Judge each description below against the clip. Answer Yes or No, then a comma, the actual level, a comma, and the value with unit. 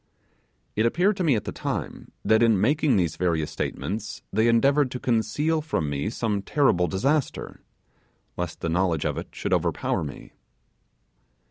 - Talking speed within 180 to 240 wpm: No, average, 155 wpm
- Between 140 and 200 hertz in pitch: No, low, 110 Hz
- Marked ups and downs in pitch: Yes, wide, 7.6 semitones